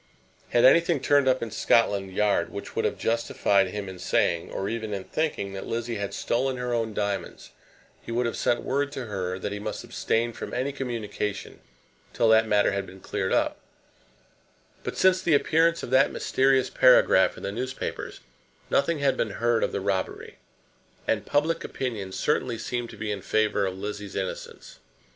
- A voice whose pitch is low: Yes, low, 115 Hz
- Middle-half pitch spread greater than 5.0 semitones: No, average, 4.5 semitones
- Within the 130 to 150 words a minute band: No, average, 180 wpm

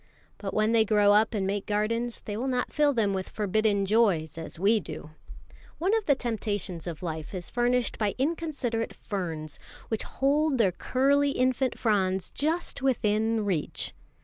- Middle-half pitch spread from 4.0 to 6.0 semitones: Yes, average, 4.5 semitones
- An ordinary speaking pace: Yes, average, 165 wpm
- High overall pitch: Yes, high, 220 Hz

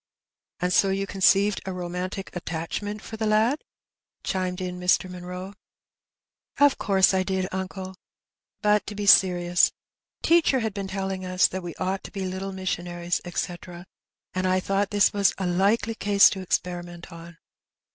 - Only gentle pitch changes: Yes, narrow, 1.8 semitones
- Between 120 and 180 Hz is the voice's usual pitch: No, high, 190 Hz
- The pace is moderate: Yes, average, 160 wpm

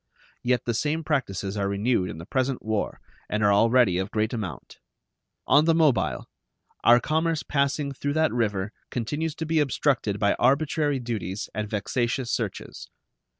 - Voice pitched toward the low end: Yes, low, 120 Hz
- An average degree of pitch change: No, wide, 6.0 semitones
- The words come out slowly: No, average, 155 wpm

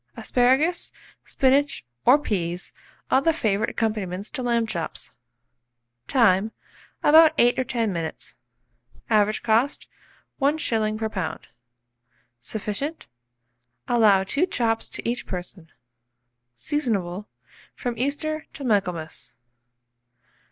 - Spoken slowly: Yes, slow, 100 wpm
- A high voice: Yes, high, 225 Hz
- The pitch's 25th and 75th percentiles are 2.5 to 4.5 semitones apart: No, wide, 5.5 semitones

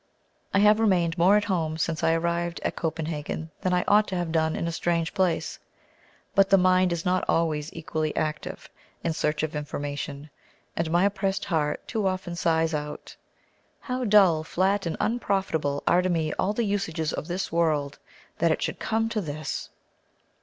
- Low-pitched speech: No, medium, 170 Hz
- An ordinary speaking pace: Yes, average, 180 wpm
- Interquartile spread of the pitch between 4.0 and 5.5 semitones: No, average, 3.3 semitones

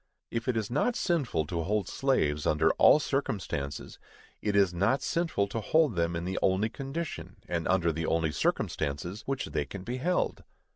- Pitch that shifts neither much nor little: No, wide, 8.2 semitones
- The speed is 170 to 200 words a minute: Yes, average, 180 wpm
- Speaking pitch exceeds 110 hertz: No, low, 100 Hz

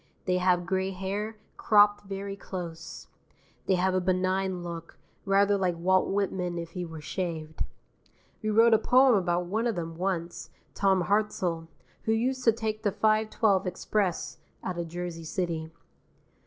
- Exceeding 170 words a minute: No, average, 155 wpm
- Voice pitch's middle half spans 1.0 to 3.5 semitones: Yes, average, 3.0 semitones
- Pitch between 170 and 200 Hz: Yes, high, 190 Hz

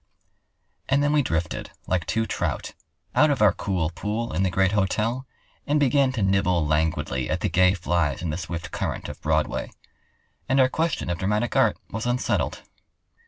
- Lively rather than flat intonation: Yes, wide, 6.3 semitones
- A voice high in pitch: No, very low, 95 Hz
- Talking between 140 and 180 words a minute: Yes, average, 175 wpm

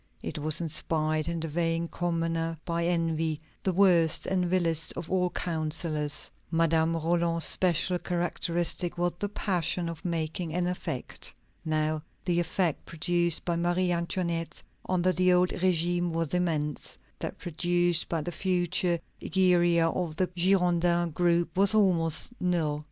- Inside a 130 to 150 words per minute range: Yes, average, 140 wpm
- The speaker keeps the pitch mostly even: Yes, narrow, 1.5 semitones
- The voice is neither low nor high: Yes, medium, 170 Hz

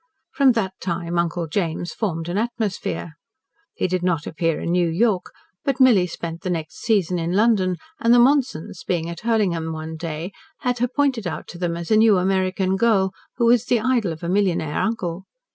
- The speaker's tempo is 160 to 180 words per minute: No, average, 195 wpm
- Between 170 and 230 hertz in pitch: Yes, medium, 185 Hz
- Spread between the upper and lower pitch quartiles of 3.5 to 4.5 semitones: No, average, 5.0 semitones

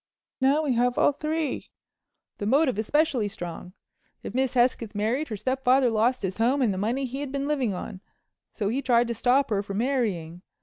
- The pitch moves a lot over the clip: No, average, 4.2 semitones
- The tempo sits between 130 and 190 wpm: Yes, average, 185 wpm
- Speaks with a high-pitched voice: Yes, high, 245 Hz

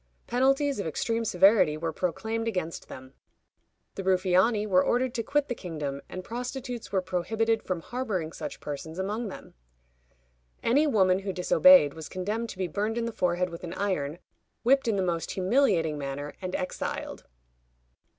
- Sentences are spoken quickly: No, average, 160 wpm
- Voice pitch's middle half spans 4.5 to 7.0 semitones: Yes, average, 5.0 semitones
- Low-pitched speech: No, high, 190 Hz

